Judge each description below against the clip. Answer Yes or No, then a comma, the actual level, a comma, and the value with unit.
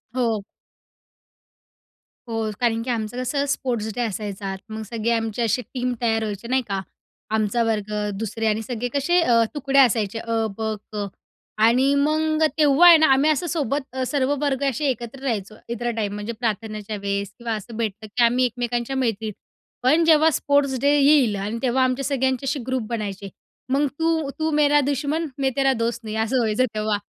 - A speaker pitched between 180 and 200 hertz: No, high, 240 Hz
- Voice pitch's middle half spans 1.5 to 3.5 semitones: No, average, 4.0 semitones